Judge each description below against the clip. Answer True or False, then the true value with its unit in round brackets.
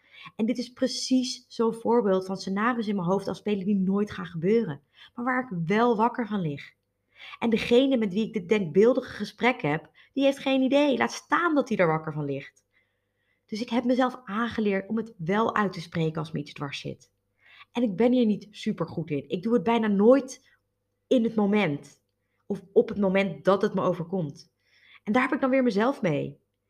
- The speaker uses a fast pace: True (210 wpm)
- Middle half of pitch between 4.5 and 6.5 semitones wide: True (5.2 semitones)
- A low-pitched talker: False (210 Hz)